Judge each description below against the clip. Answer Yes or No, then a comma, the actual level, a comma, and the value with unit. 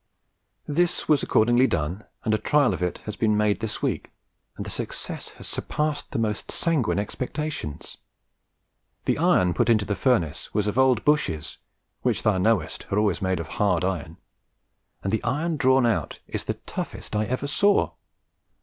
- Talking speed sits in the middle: Yes, average, 170 wpm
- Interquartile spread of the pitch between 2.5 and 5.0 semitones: No, wide, 5.6 semitones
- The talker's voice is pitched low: Yes, low, 110 Hz